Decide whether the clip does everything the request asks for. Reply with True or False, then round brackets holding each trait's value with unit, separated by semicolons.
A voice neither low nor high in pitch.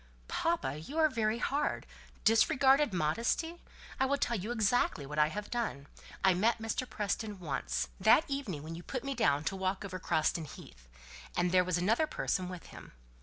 False (205 Hz)